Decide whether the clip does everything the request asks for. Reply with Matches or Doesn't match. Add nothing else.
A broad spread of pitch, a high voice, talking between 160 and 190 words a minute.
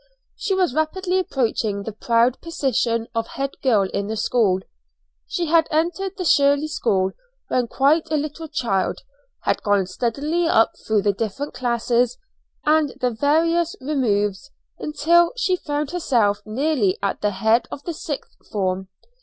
Doesn't match